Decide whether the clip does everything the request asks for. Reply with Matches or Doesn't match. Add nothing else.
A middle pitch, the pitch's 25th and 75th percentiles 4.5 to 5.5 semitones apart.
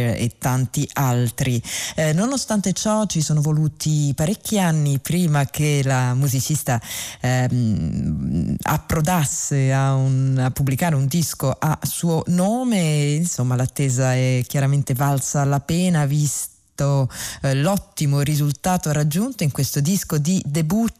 Doesn't match